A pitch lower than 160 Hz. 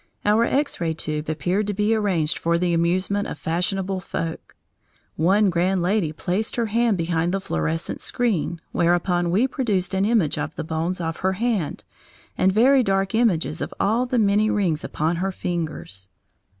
No: medium, 185 Hz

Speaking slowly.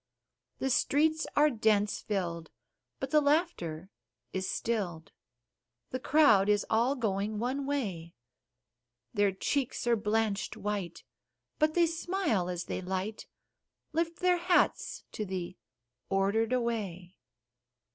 Yes: slow, 115 wpm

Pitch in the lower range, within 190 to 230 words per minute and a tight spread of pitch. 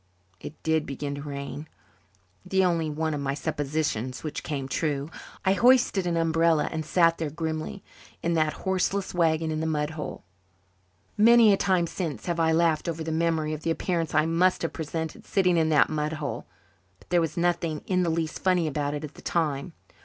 No: medium, 160 Hz; average, 195 wpm; narrow, 2.1 semitones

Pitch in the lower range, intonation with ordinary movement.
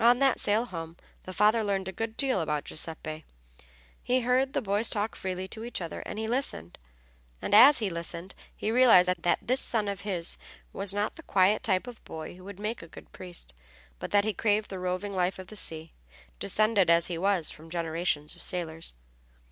No: high, 195 Hz; average, 4.3 semitones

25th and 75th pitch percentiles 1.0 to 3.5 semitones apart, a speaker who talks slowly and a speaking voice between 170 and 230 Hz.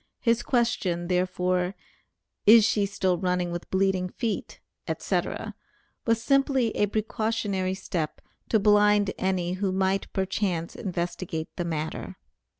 Yes: average, 2.7 semitones; slow, 120 wpm; high, 190 Hz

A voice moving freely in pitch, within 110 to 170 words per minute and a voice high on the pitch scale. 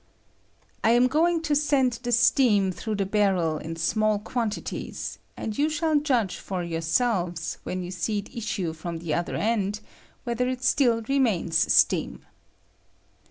Yes: wide, 5.8 semitones; average, 160 wpm; high, 215 Hz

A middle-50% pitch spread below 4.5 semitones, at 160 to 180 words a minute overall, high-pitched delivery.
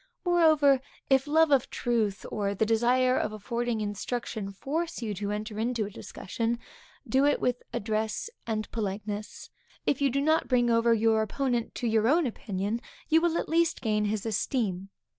Yes: average, 4.0 semitones; average, 170 wpm; high, 230 Hz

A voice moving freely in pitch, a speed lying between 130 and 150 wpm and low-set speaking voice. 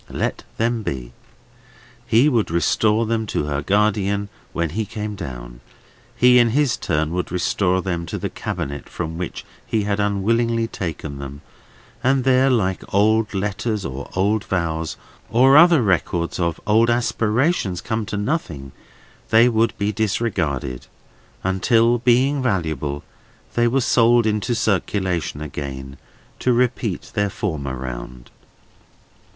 Yes: wide, 5.8 semitones; slow, 135 wpm; low, 100 Hz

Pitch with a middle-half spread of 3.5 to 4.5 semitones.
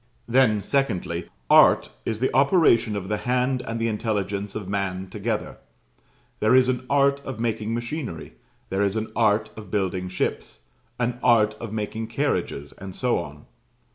Yes: average, 3.8 semitones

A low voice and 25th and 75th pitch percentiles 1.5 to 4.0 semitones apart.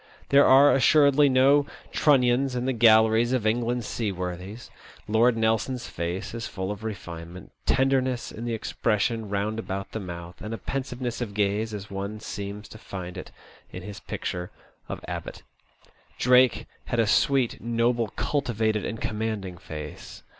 Yes: low, 110 Hz; average, 3.7 semitones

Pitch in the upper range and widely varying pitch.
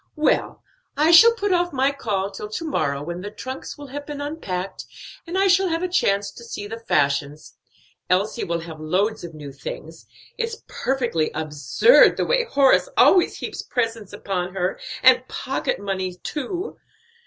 Yes: high, 220 Hz; wide, 8.8 semitones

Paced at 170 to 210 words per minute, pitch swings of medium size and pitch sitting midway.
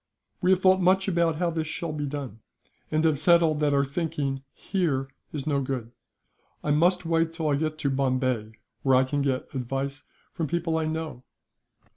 Yes: average, 180 wpm; average, 3.5 semitones; medium, 150 Hz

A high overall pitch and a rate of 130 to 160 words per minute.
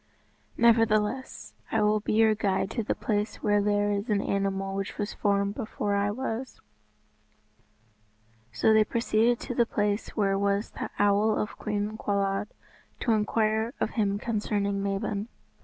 Yes: high, 210 Hz; average, 150 wpm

